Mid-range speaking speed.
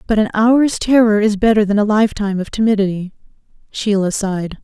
Yes: average, 170 wpm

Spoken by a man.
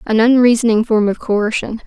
No: female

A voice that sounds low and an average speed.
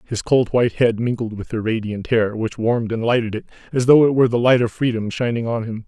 No: low, 115 Hz; fast, 255 wpm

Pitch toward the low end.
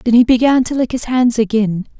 No: high, 235 Hz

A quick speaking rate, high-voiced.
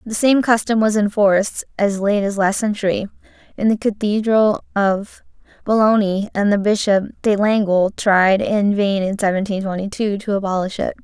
No: average, 170 wpm; high, 205 Hz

